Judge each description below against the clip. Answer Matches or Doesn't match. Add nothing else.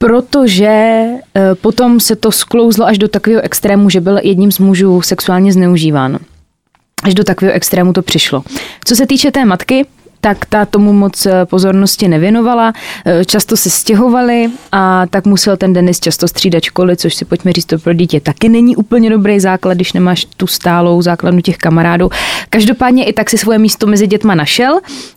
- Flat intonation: Doesn't match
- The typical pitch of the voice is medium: Doesn't match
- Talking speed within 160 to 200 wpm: Matches